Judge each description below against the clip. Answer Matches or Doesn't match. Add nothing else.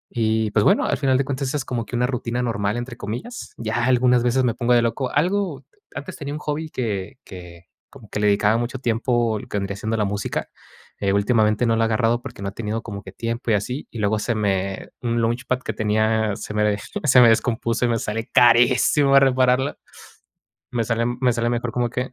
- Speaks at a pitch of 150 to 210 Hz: Doesn't match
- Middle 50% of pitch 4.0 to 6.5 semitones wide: Doesn't match